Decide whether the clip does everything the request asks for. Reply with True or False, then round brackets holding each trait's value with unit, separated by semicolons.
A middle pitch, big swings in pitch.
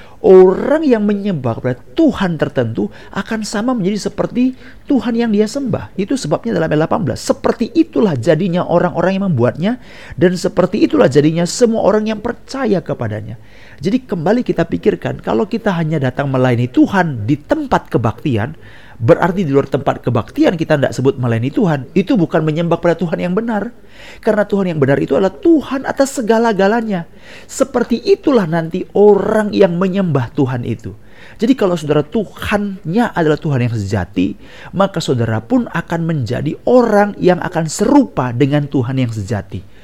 True (175 Hz; 7.9 semitones)